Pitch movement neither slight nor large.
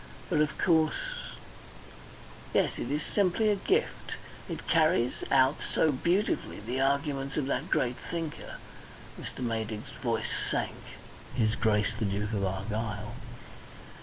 No: wide, 6.4 semitones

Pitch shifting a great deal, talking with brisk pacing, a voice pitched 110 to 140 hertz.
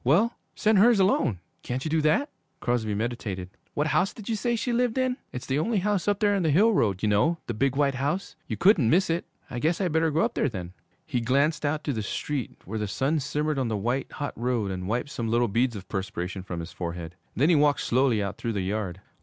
Yes: wide, 7.6 semitones; fast, 245 wpm; low, 135 Hz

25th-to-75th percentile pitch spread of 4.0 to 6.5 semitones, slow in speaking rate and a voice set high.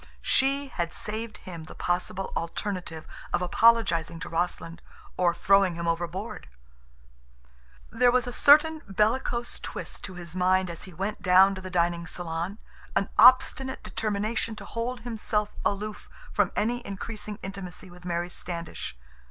No: average, 4.5 semitones; average, 145 wpm; high, 195 Hz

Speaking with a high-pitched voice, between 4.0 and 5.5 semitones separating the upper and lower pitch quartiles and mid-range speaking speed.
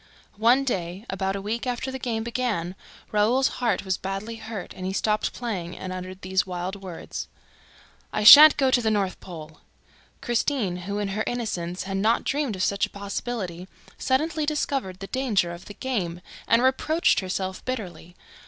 Yes: high, 205 Hz; average, 4.7 semitones; average, 170 wpm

